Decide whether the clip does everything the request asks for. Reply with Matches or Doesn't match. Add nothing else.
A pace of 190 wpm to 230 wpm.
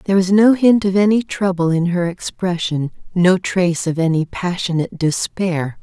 Doesn't match